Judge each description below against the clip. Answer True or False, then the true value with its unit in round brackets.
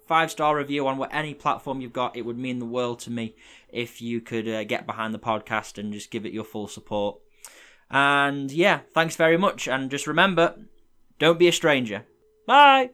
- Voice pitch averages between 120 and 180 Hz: True (135 Hz)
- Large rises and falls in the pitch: True (5.9 semitones)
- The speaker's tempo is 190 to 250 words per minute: True (205 wpm)